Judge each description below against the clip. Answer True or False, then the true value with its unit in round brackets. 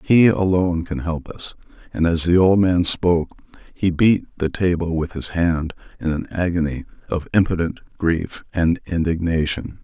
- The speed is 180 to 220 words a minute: False (160 wpm)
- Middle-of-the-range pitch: False (85 Hz)